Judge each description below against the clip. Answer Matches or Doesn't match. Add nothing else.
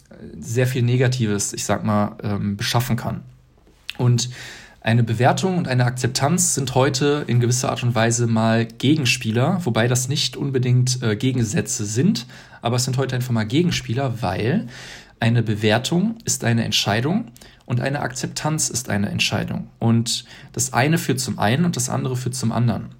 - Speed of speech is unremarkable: Matches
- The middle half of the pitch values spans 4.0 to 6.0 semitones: Doesn't match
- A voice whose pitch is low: Matches